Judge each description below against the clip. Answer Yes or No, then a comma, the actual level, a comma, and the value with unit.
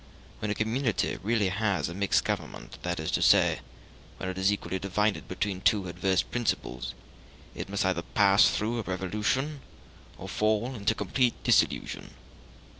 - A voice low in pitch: Yes, low, 100 Hz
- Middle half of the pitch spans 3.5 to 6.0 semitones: No, average, 2.8 semitones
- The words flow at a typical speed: Yes, average, 155 wpm